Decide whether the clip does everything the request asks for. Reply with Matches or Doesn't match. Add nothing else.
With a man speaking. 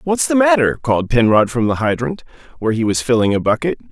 Matches